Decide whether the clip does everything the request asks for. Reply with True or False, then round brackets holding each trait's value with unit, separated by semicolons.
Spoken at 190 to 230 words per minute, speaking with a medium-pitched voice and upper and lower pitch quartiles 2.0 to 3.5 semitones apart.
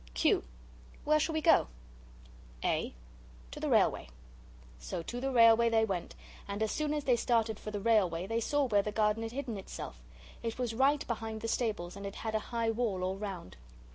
False (200 wpm; 225 Hz; 3.1 semitones)